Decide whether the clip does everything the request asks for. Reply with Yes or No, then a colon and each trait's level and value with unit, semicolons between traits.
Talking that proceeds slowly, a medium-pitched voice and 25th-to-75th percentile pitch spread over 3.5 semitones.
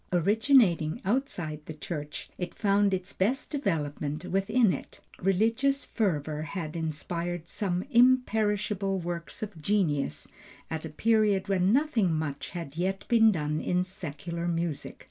Yes: slow, 130 wpm; medium, 180 Hz; average, 4.9 semitones